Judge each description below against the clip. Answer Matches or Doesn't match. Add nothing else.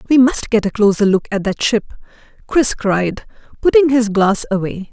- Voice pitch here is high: Matches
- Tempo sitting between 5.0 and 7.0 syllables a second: Doesn't match